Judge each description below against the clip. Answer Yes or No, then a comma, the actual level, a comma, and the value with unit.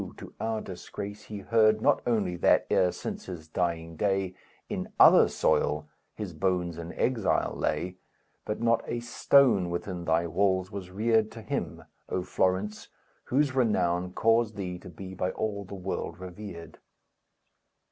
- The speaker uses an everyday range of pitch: Yes, average, 3.4 semitones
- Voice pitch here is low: Yes, very low, 95 Hz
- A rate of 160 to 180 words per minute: No, average, 150 wpm